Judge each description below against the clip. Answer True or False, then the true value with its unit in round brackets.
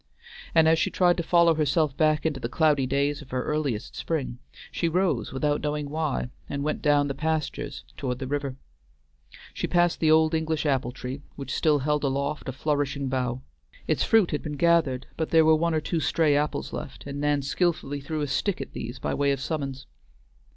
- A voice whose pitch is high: False (145 Hz)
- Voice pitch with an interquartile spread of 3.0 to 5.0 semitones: False (2.6 semitones)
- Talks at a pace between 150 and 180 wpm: False (200 wpm)